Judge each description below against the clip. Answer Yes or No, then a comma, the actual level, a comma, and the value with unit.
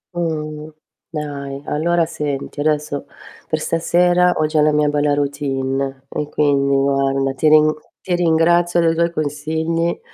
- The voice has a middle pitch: Yes, medium, 150 Hz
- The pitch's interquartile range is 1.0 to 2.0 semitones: No, average, 2.7 semitones